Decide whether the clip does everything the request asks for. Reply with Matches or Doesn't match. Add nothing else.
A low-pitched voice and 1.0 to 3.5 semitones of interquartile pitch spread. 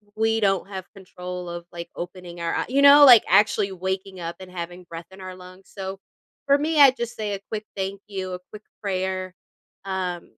Doesn't match